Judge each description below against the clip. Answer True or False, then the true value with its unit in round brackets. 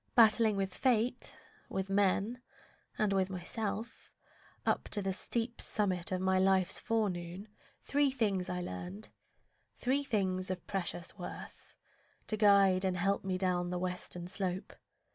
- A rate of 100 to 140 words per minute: True (135 wpm)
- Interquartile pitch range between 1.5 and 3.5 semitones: True (2.8 semitones)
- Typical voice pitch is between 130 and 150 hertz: False (195 Hz)